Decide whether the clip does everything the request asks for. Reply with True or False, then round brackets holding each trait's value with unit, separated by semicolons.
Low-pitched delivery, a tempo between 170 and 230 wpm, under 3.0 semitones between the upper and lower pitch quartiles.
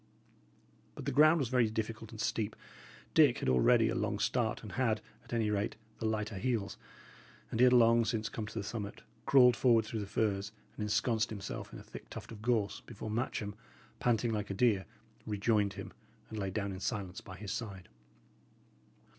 True (110 Hz; 190 wpm; 2.4 semitones)